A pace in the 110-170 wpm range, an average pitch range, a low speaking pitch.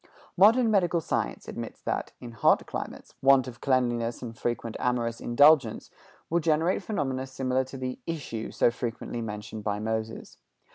Yes: average, 150 wpm; average, 4.0 semitones; low, 125 Hz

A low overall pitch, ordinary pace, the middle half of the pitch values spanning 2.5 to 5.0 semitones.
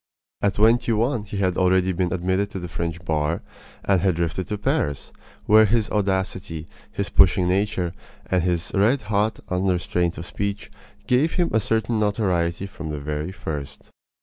Yes: very low, 95 Hz; average, 170 wpm; average, 3.3 semitones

